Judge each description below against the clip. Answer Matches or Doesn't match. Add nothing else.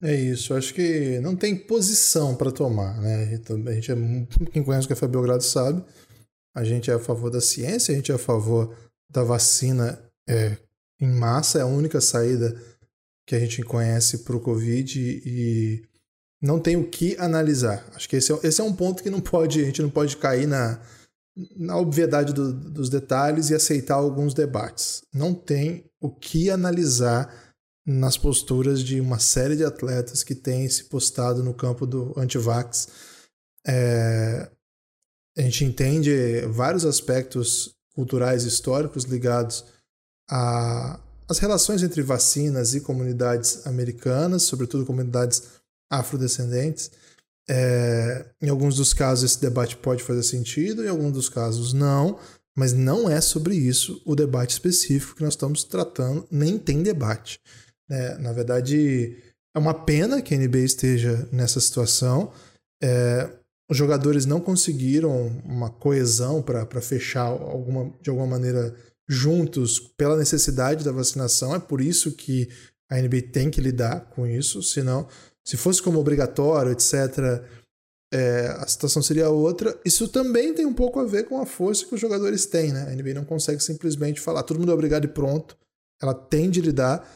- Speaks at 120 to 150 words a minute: Doesn't match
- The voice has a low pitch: Matches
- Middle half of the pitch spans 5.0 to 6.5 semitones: Doesn't match